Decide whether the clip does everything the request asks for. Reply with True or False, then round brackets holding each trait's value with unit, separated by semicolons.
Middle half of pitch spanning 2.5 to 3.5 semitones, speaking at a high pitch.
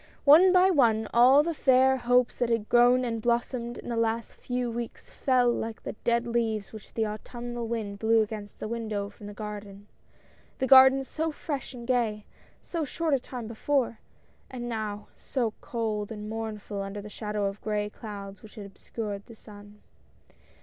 True (2.9 semitones; 230 Hz)